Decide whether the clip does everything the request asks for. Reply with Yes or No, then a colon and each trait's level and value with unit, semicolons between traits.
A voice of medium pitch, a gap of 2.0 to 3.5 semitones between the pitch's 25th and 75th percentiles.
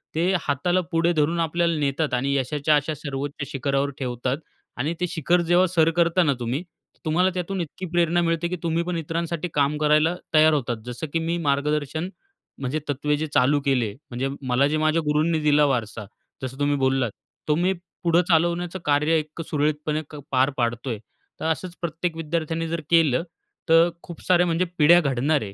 Yes: medium, 155 Hz; average, 3.2 semitones